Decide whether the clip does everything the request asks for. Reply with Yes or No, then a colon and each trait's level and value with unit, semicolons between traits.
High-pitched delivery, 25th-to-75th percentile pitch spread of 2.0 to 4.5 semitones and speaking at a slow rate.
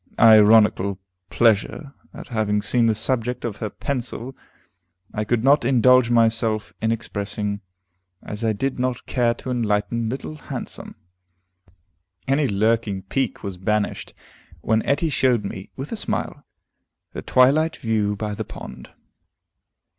No: low, 115 Hz; average, 3.3 semitones; slow, 130 wpm